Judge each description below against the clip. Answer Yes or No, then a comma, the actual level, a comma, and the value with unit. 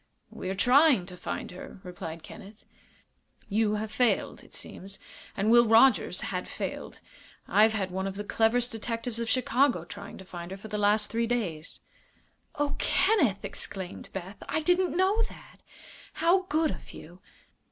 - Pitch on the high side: Yes, high, 220 Hz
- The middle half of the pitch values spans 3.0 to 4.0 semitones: No, average, 4.6 semitones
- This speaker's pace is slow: No, average, 165 wpm